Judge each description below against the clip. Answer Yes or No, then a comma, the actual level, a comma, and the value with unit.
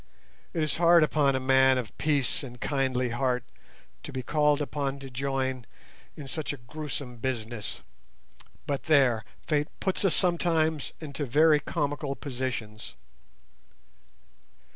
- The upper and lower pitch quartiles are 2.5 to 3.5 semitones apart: Yes, average, 2.9 semitones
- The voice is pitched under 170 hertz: Yes, medium, 140 Hz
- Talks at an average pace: No, slow, 130 wpm